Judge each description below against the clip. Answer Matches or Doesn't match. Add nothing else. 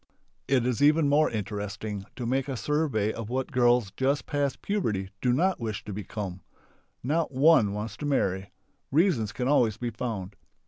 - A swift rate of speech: Doesn't match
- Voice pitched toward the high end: Doesn't match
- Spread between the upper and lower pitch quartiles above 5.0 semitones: Matches